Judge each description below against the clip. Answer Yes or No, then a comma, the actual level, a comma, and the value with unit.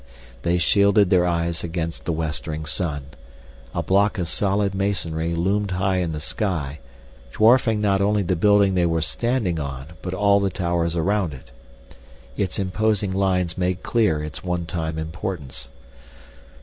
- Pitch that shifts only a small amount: No, average, 3.4 semitones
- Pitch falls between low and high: No, very low, 90 Hz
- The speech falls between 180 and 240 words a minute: No, average, 150 wpm